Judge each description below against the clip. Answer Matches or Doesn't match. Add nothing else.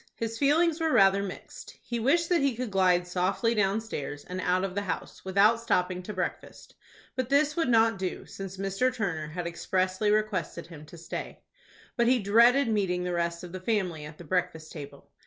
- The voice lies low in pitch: Doesn't match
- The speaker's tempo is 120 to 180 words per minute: Doesn't match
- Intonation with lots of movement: Doesn't match